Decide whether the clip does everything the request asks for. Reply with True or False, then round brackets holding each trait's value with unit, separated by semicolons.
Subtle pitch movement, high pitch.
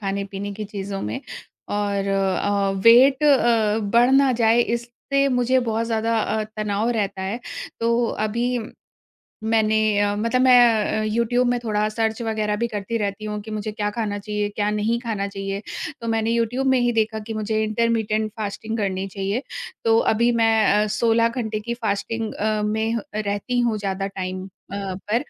True (2.2 semitones; 220 Hz)